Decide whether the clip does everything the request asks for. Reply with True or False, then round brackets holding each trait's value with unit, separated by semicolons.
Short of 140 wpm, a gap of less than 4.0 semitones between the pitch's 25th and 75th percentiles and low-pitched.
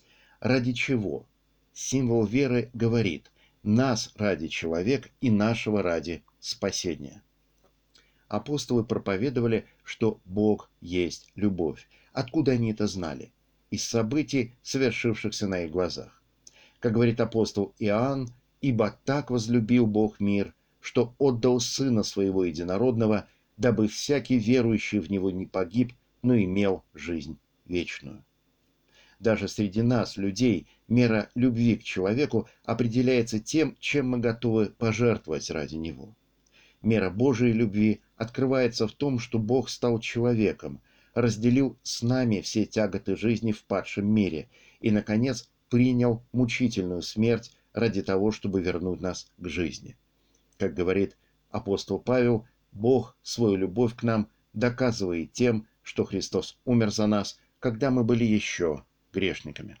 True (120 wpm; 3.3 semitones; 115 Hz)